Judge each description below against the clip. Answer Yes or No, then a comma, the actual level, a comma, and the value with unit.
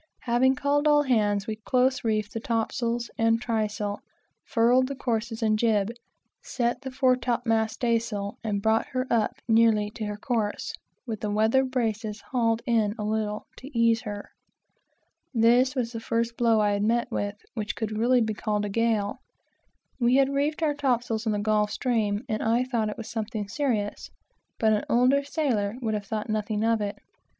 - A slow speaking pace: No, average, 180 wpm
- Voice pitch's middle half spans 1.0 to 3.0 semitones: Yes, narrow, 2.5 semitones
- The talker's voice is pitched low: No, high, 225 Hz